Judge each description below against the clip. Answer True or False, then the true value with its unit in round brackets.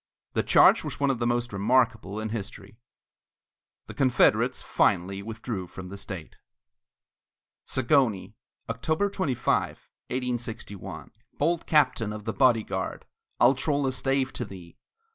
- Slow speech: True (130 wpm)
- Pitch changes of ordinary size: True (4.5 semitones)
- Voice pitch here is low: True (120 Hz)